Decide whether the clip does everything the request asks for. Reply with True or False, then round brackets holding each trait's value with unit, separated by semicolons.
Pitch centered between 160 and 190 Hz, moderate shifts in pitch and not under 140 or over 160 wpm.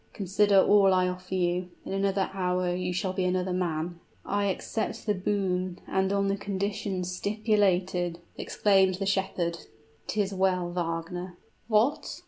False (185 Hz; 1.7 semitones; 145 wpm)